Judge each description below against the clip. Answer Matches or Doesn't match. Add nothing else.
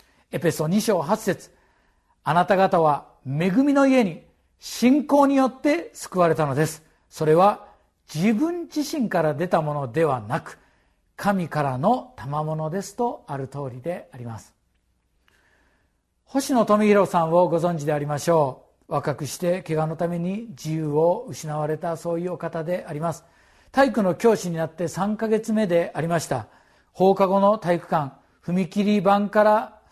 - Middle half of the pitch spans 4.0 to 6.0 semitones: Matches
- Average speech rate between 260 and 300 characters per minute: Matches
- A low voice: Doesn't match